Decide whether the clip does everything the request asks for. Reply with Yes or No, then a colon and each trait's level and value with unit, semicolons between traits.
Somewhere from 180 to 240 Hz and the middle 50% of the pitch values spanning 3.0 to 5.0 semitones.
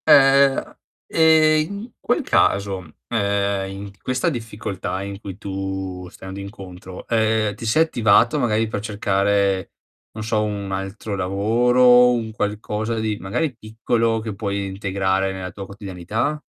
No: low, 105 Hz; average, 3.3 semitones